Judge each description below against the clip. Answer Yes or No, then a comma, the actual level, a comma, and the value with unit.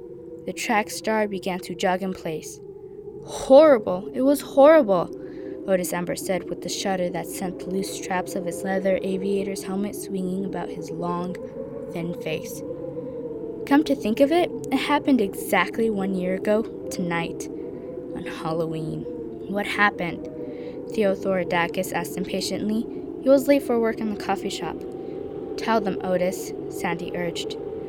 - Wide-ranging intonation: Yes, wide, 7.9 semitones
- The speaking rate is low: No, average, 145 wpm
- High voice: Yes, high, 205 Hz